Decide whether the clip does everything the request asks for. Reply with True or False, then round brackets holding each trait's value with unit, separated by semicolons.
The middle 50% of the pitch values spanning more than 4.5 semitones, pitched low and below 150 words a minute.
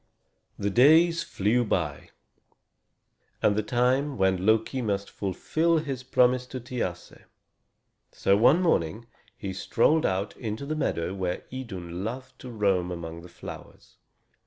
True (5.4 semitones; 110 Hz; 135 wpm)